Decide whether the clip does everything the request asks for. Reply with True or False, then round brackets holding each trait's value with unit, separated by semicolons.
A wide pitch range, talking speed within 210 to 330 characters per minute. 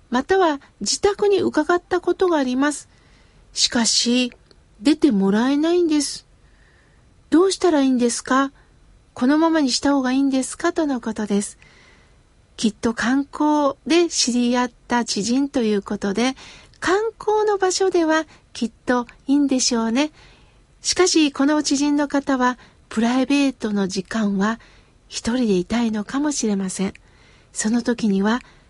False (4.8 semitones; 285 characters per minute)